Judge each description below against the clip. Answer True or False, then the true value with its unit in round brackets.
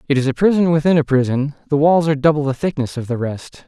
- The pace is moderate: False (260 wpm)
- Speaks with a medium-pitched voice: True (145 Hz)